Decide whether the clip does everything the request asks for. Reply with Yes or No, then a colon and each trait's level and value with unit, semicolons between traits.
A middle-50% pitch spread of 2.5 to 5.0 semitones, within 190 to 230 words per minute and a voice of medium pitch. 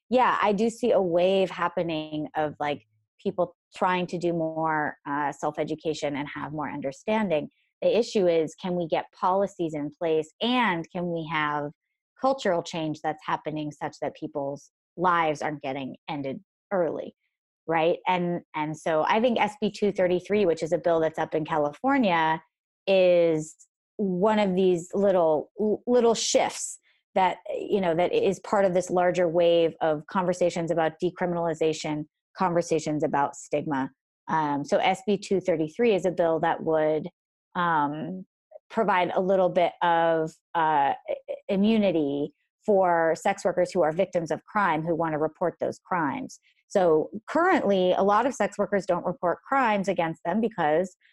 No: average, 4.0 semitones; average, 155 wpm; medium, 175 Hz